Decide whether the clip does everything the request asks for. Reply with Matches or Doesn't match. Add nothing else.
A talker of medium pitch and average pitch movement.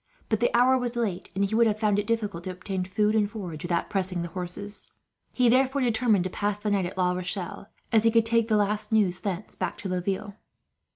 Doesn't match